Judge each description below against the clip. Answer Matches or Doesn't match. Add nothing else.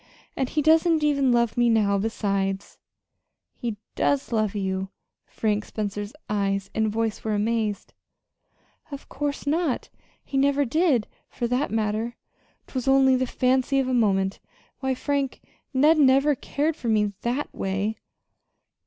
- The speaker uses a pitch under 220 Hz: Doesn't match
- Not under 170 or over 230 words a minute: Doesn't match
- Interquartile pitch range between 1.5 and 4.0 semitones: Doesn't match